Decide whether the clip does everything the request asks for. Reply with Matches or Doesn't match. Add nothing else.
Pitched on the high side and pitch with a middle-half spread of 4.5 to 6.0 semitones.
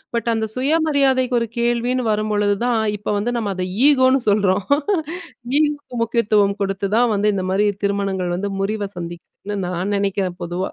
Doesn't match